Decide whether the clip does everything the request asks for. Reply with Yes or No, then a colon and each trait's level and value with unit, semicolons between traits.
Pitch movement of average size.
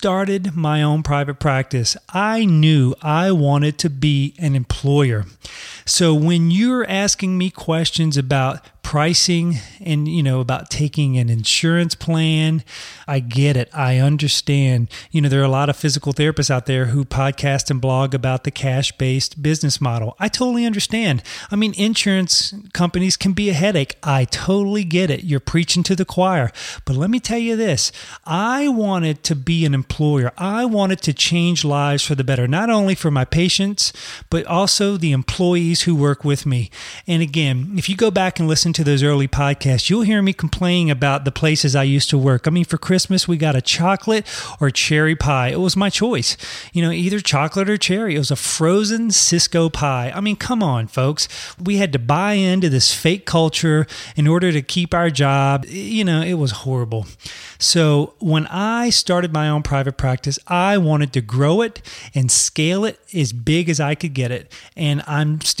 Yes: average, 4.9 semitones